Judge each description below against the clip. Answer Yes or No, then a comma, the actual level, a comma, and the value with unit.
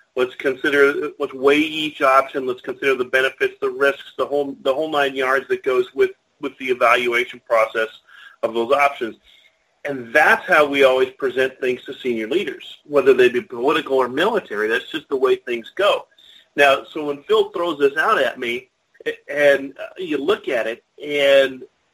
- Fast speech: No, average, 180 wpm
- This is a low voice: No, medium, 145 Hz